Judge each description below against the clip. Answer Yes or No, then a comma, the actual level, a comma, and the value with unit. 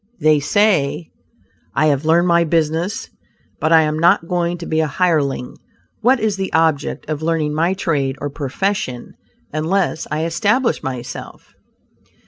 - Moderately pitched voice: Yes, medium, 160 Hz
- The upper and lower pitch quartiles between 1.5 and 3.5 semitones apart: Yes, average, 3.0 semitones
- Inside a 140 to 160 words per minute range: Yes, average, 145 wpm